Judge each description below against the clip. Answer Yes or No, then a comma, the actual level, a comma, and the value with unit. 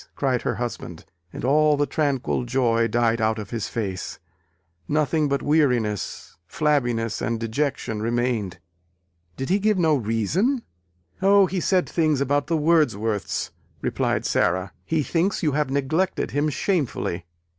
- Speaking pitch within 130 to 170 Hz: Yes, low, 135 Hz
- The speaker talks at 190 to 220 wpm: No, average, 140 wpm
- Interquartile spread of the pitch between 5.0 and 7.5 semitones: Yes, average, 5.3 semitones